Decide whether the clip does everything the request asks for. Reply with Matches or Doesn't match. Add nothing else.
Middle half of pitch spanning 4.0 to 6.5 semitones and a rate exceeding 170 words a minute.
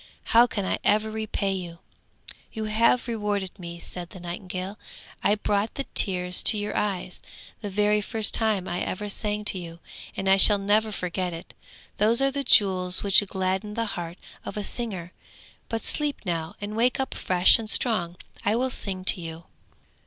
Doesn't match